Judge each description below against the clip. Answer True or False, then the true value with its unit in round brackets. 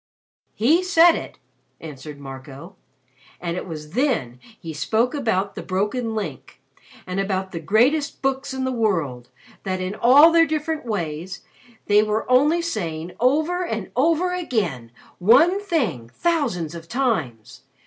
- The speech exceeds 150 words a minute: False (140 wpm)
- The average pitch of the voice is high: True (215 Hz)